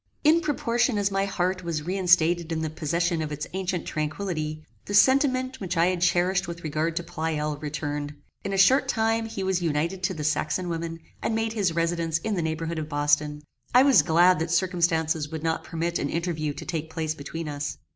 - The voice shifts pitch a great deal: No, average, 3.3 semitones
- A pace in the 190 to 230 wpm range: Yes, average, 200 wpm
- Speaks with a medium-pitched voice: Yes, medium, 170 Hz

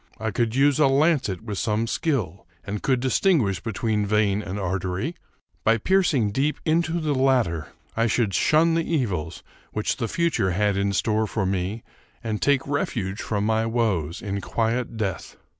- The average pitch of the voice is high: No, low, 110 Hz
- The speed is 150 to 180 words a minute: Yes, average, 165 wpm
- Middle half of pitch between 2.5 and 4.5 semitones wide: No, wide, 5.4 semitones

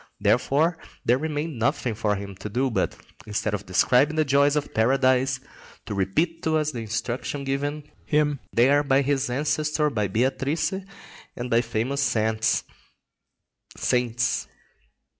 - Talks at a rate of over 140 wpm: No, slow, 135 wpm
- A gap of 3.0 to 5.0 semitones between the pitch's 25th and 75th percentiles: Yes, average, 4.1 semitones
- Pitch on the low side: Yes, low, 130 Hz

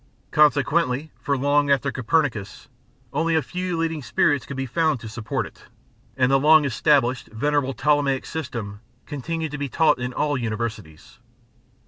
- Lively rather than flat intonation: No, average, 3.4 semitones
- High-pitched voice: No, medium, 140 Hz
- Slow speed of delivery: No, average, 150 wpm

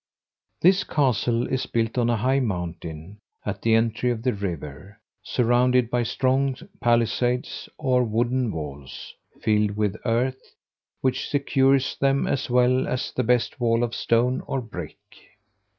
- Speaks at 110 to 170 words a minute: Yes, average, 140 wpm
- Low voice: Yes, low, 120 Hz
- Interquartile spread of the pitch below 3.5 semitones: Yes, average, 3.0 semitones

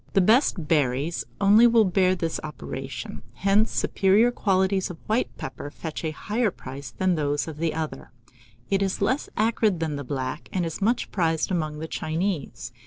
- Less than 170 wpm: No, average, 175 wpm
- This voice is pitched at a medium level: Yes, medium, 170 Hz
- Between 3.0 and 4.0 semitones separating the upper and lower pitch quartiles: No, average, 4.8 semitones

